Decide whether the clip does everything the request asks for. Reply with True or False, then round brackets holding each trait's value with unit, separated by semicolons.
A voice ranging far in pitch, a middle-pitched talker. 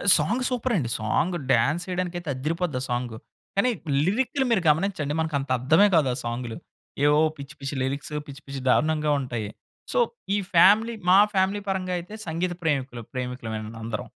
True (6.1 semitones; 150 Hz)